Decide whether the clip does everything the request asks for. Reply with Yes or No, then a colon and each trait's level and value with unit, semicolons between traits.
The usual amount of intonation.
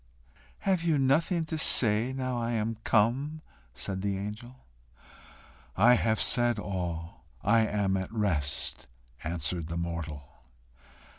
No: wide, 6.0 semitones